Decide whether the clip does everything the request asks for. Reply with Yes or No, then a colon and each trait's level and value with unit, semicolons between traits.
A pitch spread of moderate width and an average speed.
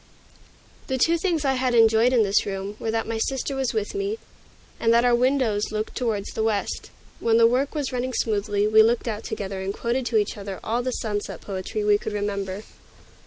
No: average, 3.4 semitones; fast, 210 wpm